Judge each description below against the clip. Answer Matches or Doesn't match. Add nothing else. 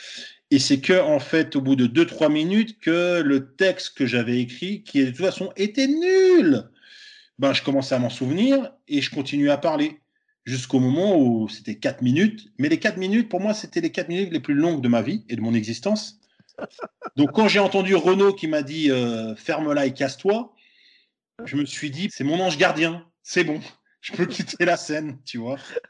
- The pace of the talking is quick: Doesn't match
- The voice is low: Doesn't match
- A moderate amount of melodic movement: Doesn't match